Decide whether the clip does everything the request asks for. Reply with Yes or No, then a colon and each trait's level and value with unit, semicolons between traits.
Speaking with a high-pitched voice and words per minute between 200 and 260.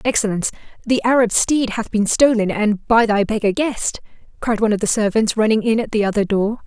Yes: high, 220 Hz; fast, 205 wpm